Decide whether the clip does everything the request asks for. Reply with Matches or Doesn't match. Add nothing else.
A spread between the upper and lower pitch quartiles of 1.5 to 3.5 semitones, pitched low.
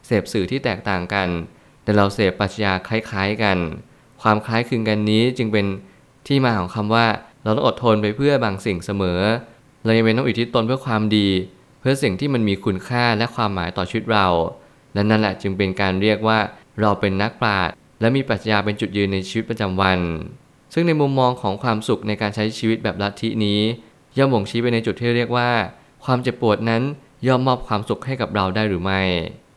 Matches